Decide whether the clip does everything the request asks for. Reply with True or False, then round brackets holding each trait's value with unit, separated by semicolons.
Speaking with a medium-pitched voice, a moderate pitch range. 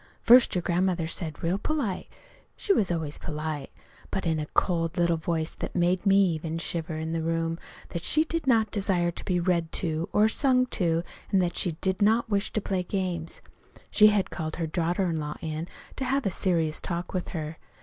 True (175 Hz; 3.3 semitones)